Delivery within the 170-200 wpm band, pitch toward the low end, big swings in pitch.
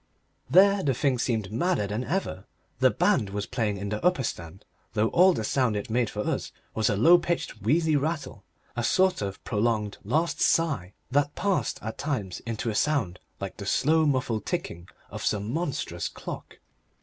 Yes: average, 180 wpm; low, 120 Hz; wide, 7.1 semitones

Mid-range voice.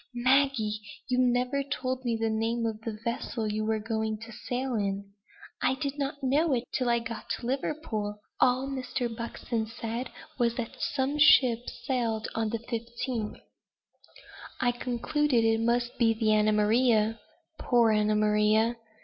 No: high, 235 Hz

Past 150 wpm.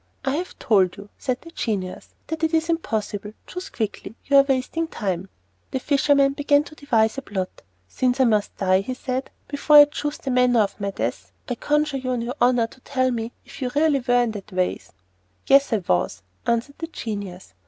Yes: fast, 205 wpm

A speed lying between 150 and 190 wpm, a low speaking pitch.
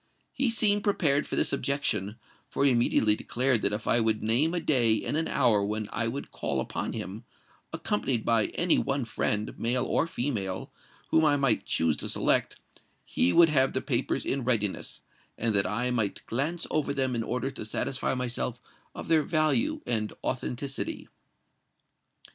Yes: average, 170 wpm; low, 125 Hz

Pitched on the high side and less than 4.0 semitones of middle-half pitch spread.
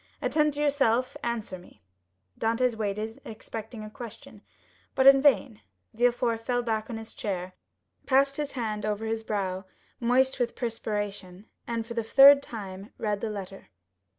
Yes: high, 225 Hz; average, 3.1 semitones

